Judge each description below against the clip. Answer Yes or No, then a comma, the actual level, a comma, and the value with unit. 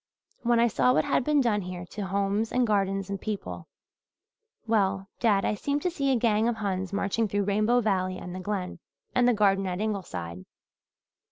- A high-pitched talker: Yes, high, 205 Hz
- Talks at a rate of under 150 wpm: No, average, 190 wpm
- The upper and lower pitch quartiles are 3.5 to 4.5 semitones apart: No, average, 3.1 semitones